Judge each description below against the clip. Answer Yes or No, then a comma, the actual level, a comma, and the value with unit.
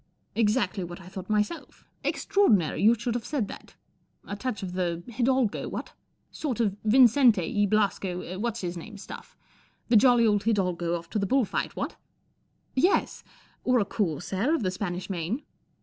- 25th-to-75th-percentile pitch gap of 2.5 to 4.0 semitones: No, average, 4.5 semitones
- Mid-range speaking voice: No, high, 210 Hz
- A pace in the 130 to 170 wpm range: No, average, 180 wpm